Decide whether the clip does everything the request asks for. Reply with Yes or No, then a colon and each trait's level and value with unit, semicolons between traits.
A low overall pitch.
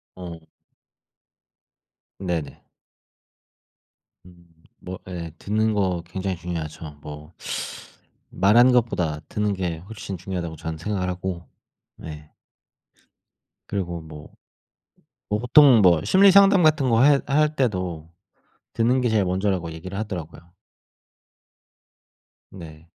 Yes: very low, 90 Hz